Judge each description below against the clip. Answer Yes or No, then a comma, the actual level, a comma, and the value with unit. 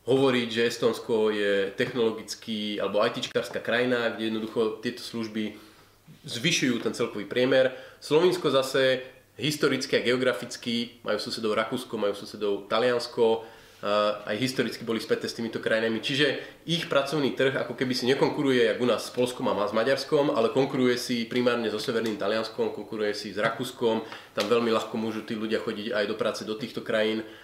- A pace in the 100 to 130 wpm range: No, fast, 165 wpm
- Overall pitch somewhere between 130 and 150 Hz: No, low, 115 Hz